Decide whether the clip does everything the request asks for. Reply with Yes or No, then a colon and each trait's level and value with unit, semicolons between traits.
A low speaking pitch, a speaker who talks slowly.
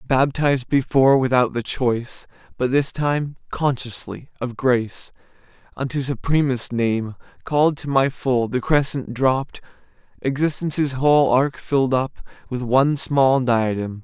Yes: low, 130 Hz; slow, 130 wpm